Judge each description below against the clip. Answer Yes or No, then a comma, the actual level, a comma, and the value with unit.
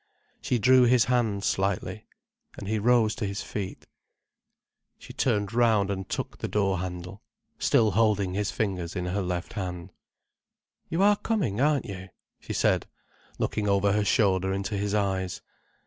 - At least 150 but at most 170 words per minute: Yes, average, 155 wpm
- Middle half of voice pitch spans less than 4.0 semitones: Yes, average, 2.9 semitones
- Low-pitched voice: Yes, low, 100 Hz